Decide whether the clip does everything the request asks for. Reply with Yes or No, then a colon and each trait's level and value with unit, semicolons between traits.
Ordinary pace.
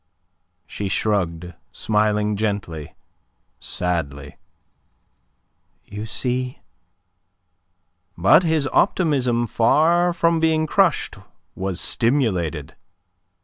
No: slow, 70 wpm